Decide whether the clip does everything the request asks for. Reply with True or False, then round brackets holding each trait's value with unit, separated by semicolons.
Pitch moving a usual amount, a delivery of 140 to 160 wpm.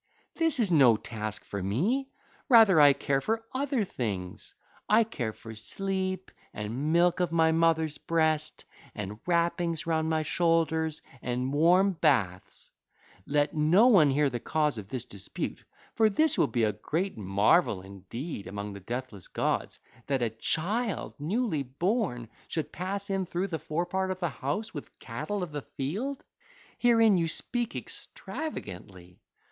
False (7.7 semitones; 150 wpm)